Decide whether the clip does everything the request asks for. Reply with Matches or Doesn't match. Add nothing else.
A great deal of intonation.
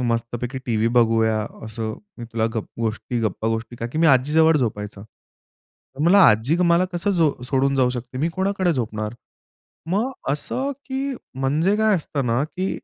Matches